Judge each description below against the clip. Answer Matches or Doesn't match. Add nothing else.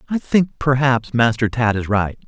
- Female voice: Doesn't match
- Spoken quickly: Doesn't match